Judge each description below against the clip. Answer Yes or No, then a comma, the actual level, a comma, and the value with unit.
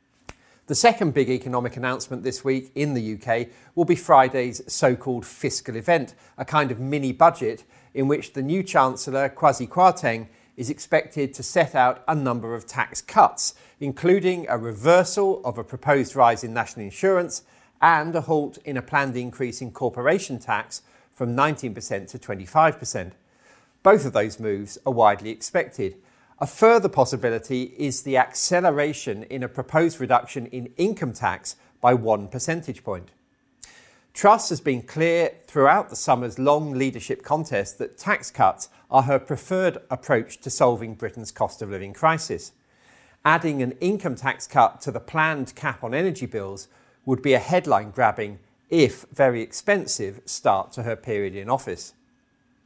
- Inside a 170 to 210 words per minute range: No, average, 155 wpm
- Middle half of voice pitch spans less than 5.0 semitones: Yes, average, 4.4 semitones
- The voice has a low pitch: Yes, low, 130 Hz